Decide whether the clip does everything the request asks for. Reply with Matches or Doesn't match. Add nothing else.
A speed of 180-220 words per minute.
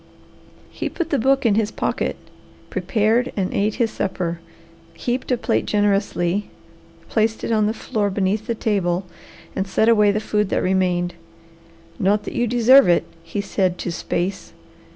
Doesn't match